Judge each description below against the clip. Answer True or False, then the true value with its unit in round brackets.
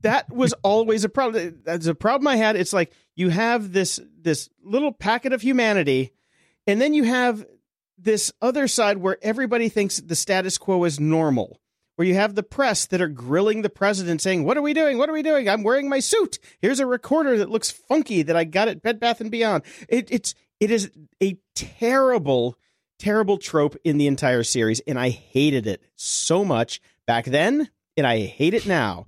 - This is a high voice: True (205 Hz)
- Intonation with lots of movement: True (6.3 semitones)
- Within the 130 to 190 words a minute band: False (200 wpm)